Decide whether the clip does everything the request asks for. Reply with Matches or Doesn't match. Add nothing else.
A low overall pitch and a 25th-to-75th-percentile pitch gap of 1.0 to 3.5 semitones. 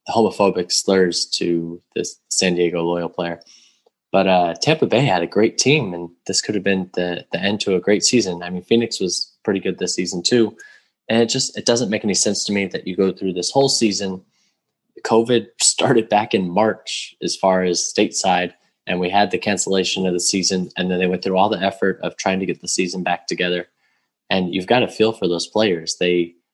Matches